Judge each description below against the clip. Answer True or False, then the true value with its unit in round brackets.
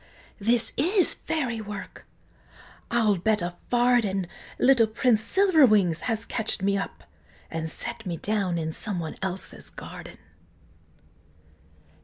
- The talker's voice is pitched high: True (215 Hz)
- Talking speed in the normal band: False (120 wpm)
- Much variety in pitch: False (4.1 semitones)